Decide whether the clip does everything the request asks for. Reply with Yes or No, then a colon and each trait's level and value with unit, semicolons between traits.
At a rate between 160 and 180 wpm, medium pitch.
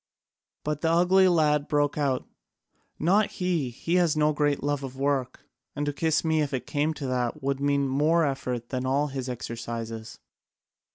Yes: average, 175 wpm; medium, 145 Hz